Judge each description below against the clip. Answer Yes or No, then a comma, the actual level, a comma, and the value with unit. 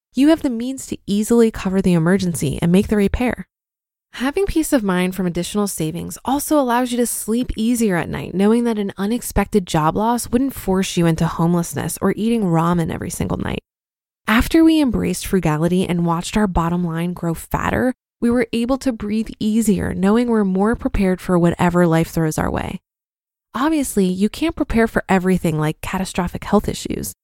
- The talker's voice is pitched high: Yes, high, 200 Hz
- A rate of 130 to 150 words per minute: No, average, 180 wpm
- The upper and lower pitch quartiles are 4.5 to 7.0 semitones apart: Yes, average, 5.2 semitones